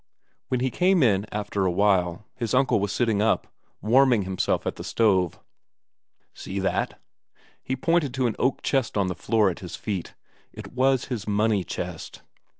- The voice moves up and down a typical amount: Yes, average, 4.6 semitones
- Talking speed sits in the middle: Yes, average, 170 wpm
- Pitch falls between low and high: No, low, 110 Hz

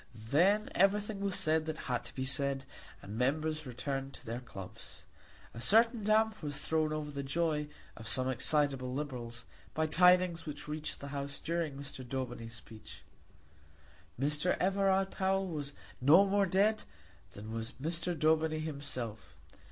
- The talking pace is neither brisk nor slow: Yes, average, 150 wpm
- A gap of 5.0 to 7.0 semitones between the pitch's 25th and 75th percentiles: Yes, wide, 5.5 semitones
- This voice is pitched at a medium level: Yes, medium, 150 Hz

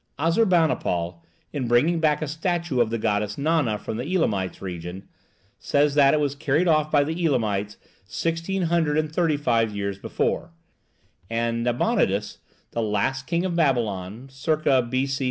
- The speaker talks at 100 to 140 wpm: Yes, slow, 135 wpm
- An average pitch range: No, wide, 6.5 semitones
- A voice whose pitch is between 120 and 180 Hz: Yes, low, 135 Hz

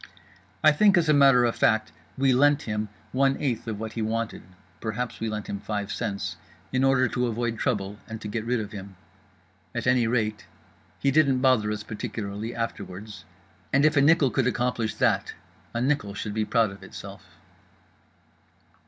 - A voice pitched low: Yes, low, 115 Hz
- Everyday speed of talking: Yes, average, 175 wpm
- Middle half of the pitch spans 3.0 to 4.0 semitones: Yes, average, 3.6 semitones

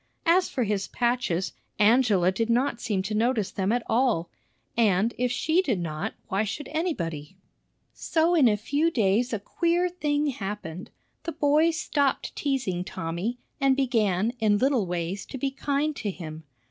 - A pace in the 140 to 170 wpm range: Yes, average, 160 wpm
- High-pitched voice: Yes, high, 230 Hz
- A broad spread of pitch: Yes, wide, 6.6 semitones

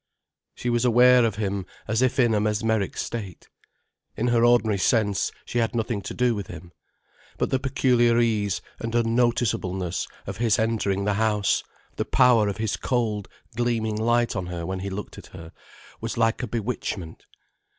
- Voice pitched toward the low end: Yes, low, 110 Hz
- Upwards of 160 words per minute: Yes, average, 170 wpm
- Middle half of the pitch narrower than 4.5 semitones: Yes, average, 2.8 semitones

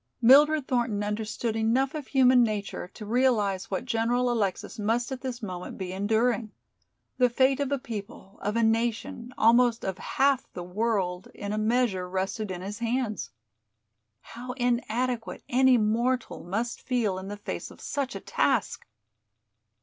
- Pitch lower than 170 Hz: No, high, 230 Hz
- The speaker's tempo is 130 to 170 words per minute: Yes, average, 155 wpm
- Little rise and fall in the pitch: No, average, 3.4 semitones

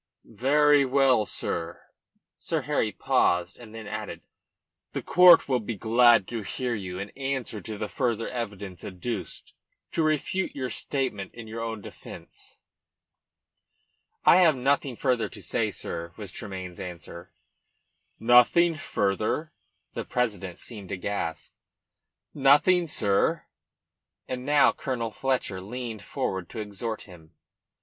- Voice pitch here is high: No, low, 115 Hz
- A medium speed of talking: No, slow, 125 wpm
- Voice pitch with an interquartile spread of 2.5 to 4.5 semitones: No, average, 5.1 semitones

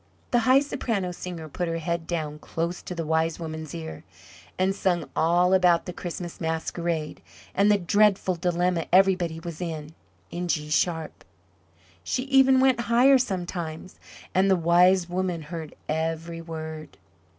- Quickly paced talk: No, average, 150 wpm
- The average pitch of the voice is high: No, medium, 175 Hz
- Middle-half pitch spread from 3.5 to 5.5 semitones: No, narrow, 2.6 semitones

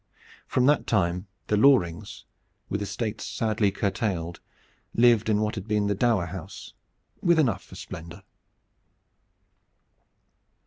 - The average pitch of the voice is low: Yes, low, 105 Hz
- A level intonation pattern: No, average, 3.6 semitones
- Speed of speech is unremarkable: No, slow, 120 wpm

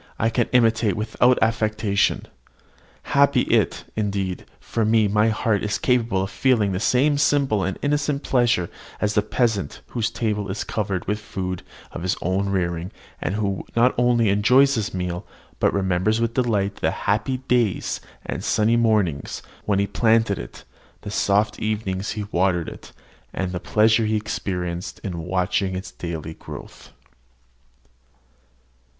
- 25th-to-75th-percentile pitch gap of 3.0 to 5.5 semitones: Yes, average, 3.4 semitones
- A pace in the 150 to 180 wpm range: Yes, average, 155 wpm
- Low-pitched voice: Yes, low, 105 Hz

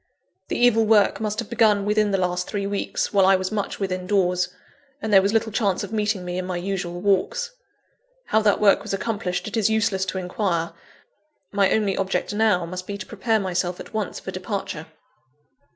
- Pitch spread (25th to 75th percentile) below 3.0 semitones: Yes, narrow, 2.6 semitones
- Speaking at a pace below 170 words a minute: No, average, 200 wpm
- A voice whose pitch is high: Yes, high, 200 Hz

